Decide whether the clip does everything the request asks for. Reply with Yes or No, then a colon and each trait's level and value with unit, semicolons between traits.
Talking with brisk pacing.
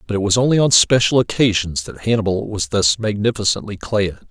No: average, 180 wpm